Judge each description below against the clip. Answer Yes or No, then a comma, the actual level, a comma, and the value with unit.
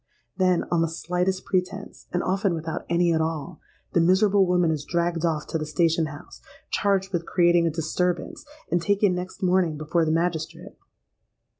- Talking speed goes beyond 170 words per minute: No, average, 160 wpm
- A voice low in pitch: No, medium, 175 Hz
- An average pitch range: No, narrow, 2.0 semitones